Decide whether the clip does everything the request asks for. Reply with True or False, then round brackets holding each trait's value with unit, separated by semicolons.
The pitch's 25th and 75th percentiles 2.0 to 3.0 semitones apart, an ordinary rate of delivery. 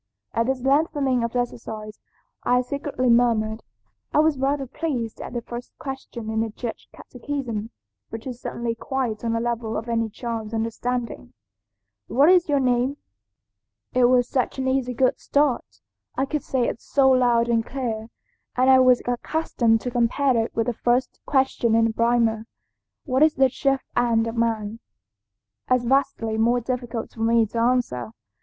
True (2.5 semitones; 165 wpm)